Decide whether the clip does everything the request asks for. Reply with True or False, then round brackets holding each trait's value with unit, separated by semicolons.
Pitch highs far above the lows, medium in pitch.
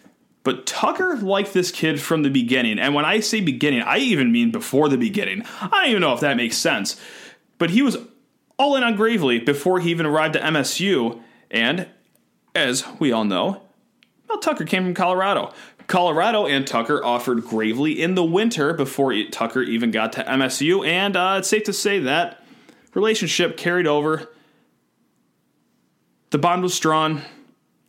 True (6.9 semitones; 175 Hz)